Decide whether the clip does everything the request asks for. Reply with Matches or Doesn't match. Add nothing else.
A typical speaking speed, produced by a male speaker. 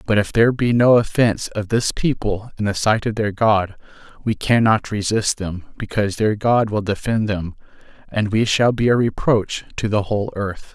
Matches